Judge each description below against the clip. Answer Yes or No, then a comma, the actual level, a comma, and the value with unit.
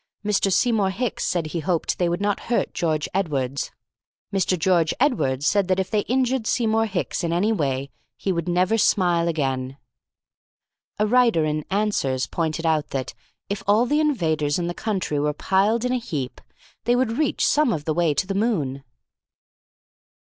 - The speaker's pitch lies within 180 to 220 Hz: Yes, medium, 185 Hz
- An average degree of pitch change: No, wide, 5.9 semitones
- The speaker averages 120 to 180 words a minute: Yes, average, 175 wpm